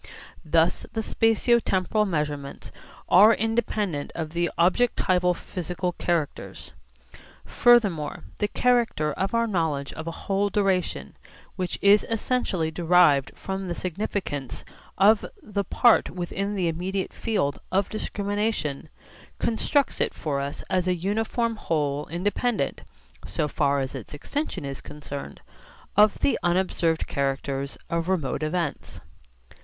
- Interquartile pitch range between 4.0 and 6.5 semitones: Yes, average, 5.2 semitones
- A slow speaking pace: Yes, slow, 125 wpm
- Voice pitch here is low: No, medium, 180 Hz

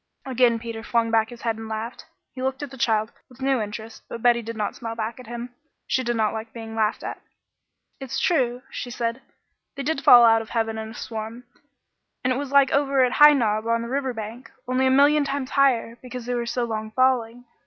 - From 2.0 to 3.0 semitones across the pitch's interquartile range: Yes, narrow, 2.6 semitones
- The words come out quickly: Yes, fast, 230 wpm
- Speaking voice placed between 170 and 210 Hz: No, high, 235 Hz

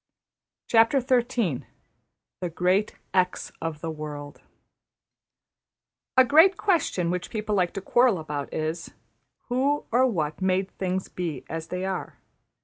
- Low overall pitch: No, medium, 185 Hz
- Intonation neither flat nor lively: No, wide, 6.6 semitones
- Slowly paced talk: Yes, slow, 120 wpm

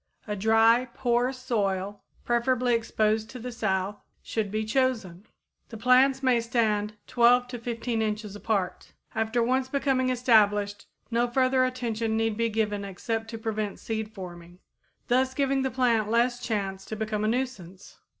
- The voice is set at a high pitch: Yes, high, 225 Hz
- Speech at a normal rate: Yes, average, 150 wpm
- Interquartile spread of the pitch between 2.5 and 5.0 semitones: Yes, average, 2.8 semitones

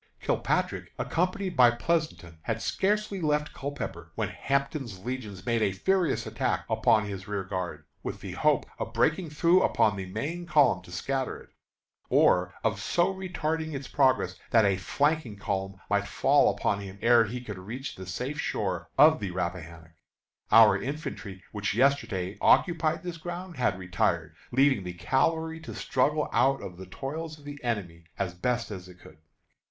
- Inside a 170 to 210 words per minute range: No, average, 160 wpm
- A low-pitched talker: Yes, low, 120 Hz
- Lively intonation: Yes, wide, 8.3 semitones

